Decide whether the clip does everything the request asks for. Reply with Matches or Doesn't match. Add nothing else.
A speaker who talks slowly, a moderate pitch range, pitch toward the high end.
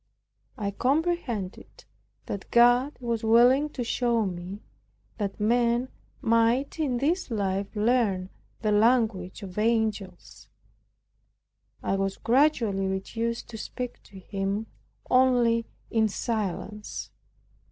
Matches